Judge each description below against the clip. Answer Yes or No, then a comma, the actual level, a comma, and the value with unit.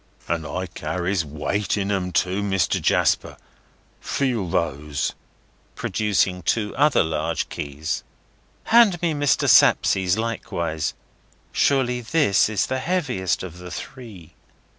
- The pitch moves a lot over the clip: Yes, wide, 6.2 semitones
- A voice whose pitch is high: No, very low, 95 Hz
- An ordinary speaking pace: No, slow, 120 wpm